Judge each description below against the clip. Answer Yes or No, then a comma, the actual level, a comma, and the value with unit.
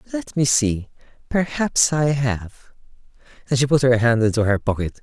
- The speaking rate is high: No, average, 155 wpm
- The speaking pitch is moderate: No, low, 125 Hz